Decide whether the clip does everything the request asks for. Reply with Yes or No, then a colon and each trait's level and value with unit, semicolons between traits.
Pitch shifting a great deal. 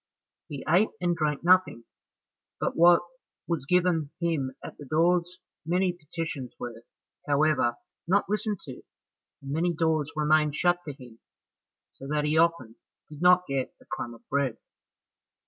No: average, 3.9 semitones